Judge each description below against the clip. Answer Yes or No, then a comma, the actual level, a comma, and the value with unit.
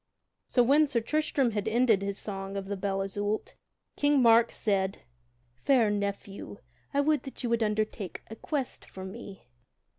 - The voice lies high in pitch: Yes, high, 215 Hz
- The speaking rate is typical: Yes, average, 160 wpm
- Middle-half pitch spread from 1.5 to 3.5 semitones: No, average, 4.2 semitones